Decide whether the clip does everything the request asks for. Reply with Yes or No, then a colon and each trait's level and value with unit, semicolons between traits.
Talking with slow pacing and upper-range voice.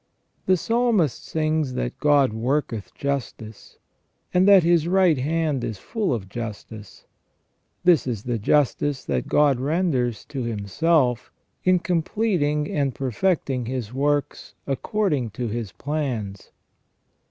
No: slow, 125 wpm; medium, 140 Hz